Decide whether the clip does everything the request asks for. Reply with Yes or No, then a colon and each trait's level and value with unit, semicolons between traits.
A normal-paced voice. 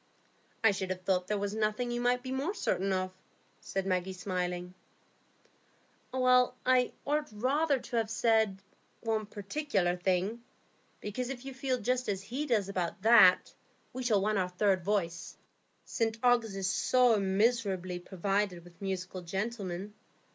Yes: average, 145 wpm